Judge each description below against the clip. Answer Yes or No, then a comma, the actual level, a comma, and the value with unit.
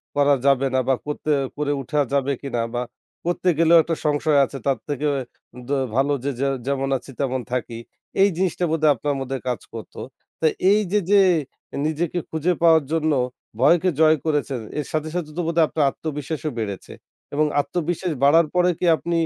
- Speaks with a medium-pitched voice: Yes, medium, 150 Hz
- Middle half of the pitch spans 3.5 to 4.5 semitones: No, average, 3.1 semitones